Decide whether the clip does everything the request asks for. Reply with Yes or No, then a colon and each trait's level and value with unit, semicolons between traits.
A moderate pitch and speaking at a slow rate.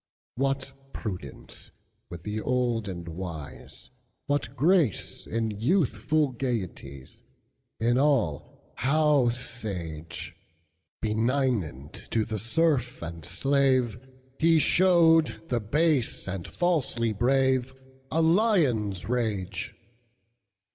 No: low, 120 Hz; slow, 80 wpm